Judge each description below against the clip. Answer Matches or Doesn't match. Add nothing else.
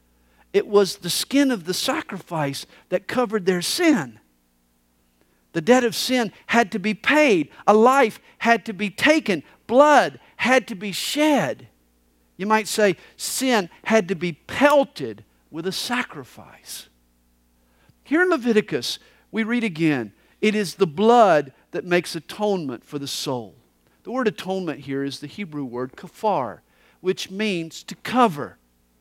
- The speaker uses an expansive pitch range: Matches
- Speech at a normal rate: Matches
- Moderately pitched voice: Doesn't match